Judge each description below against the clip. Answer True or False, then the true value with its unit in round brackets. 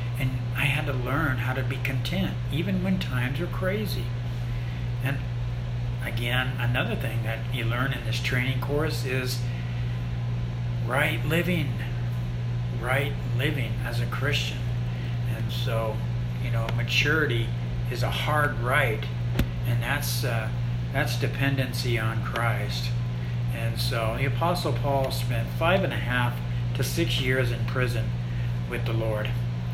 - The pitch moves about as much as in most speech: False (1.2 semitones)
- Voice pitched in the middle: False (120 Hz)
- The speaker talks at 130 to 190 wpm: True (135 wpm)